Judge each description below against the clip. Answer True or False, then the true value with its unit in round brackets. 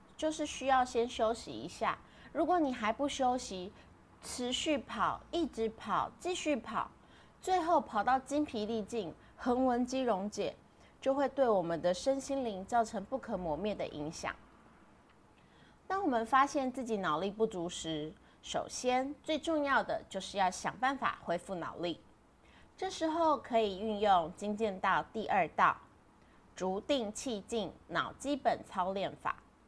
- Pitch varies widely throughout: True (6.0 semitones)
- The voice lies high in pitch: True (235 Hz)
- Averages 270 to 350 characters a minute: False (215 characters per minute)